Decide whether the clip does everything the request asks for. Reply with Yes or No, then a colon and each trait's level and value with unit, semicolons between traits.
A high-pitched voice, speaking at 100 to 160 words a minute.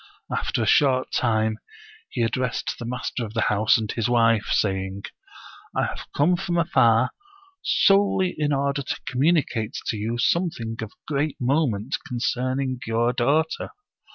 No: low, 125 Hz; average, 150 wpm